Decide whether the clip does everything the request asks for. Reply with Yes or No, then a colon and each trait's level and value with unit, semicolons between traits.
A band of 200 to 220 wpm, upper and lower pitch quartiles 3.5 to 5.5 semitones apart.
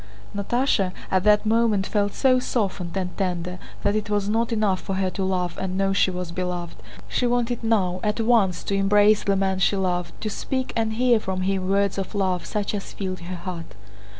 No: fast, 205 wpm; average, 2.7 semitones